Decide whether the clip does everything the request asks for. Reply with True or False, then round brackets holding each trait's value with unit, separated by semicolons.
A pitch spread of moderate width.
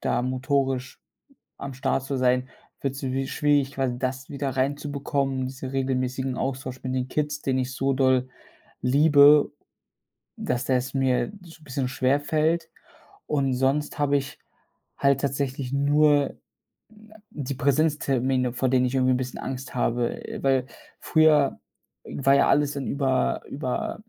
False (1.6 semitones)